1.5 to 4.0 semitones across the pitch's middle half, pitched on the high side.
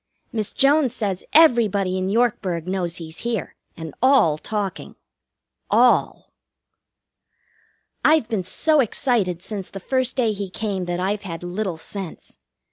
No: average, 4.7 semitones; high, 200 Hz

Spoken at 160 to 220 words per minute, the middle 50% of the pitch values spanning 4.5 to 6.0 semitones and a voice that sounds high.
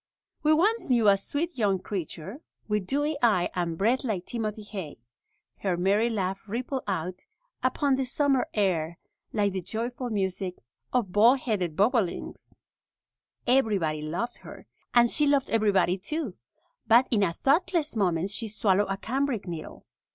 No: average, 145 wpm; average, 5.3 semitones; high, 215 Hz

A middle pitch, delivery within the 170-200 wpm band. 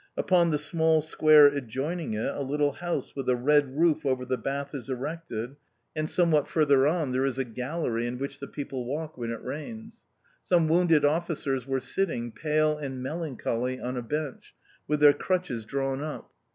Yes: medium, 145 Hz; average, 180 wpm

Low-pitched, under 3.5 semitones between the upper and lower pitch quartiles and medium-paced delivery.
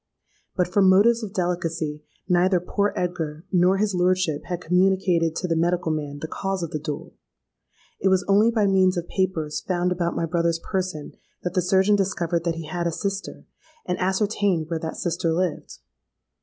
No: medium, 180 Hz; narrow, 2.4 semitones; average, 180 wpm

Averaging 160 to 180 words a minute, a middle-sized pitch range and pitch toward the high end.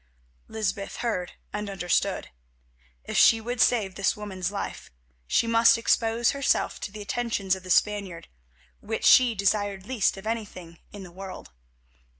No: average, 150 wpm; average, 3.2 semitones; high, 205 Hz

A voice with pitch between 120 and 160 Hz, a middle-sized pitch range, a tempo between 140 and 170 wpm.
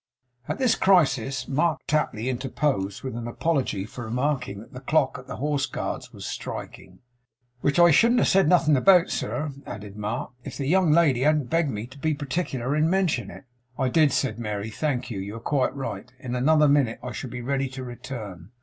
No: low, 135 Hz; average, 4.1 semitones; average, 200 wpm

